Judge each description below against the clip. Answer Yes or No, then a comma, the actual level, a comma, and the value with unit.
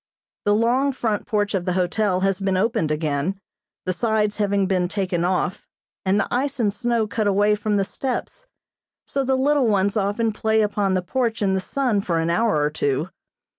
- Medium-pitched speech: No, high, 205 Hz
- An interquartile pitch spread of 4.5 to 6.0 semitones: No, average, 3.3 semitones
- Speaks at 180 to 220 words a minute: Yes, average, 195 wpm